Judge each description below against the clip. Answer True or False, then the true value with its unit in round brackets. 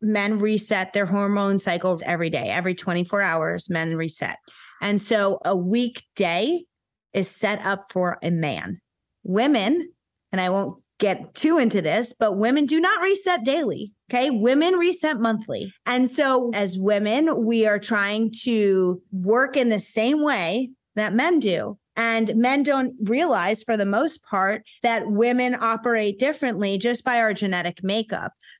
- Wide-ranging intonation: False (4.1 semitones)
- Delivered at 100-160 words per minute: True (155 wpm)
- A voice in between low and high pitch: False (220 Hz)